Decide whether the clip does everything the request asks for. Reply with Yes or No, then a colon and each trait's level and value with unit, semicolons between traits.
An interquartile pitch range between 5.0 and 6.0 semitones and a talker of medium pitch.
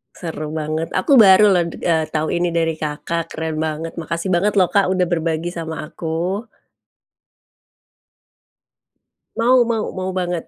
No: average, 2.7 semitones; medium, 170 Hz